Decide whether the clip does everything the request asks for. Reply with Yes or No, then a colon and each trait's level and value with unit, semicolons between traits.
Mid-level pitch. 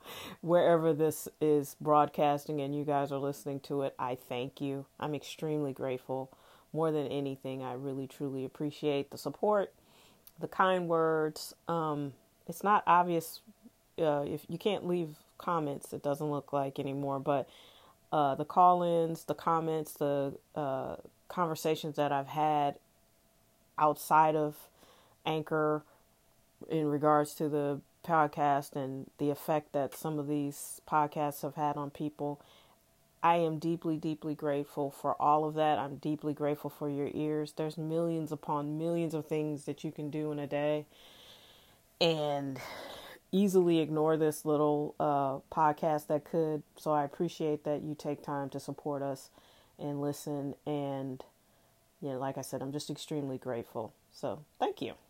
Yes: medium, 150 Hz